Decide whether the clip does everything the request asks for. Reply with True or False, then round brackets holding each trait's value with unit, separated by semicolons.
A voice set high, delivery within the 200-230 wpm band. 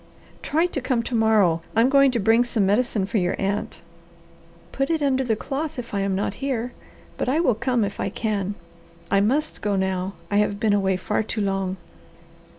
True (220 Hz; 205 wpm)